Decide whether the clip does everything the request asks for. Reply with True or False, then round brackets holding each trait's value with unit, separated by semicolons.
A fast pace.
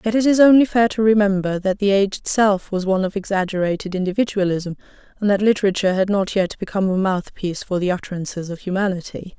False (190 wpm)